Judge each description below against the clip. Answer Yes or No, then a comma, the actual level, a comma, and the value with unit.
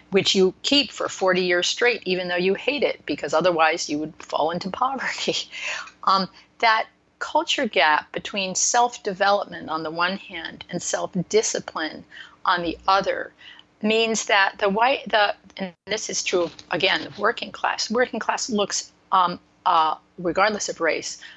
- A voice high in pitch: Yes, high, 195 Hz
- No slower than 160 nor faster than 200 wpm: No, average, 150 wpm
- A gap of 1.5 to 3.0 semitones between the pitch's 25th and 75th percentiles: No, average, 3.9 semitones